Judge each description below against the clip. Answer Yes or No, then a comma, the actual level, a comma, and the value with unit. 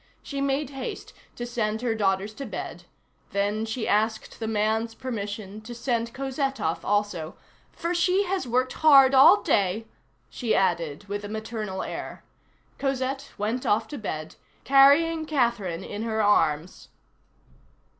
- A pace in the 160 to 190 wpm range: No, average, 145 wpm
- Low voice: No, high, 225 Hz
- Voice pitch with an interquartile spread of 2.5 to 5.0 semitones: Yes, average, 4.7 semitones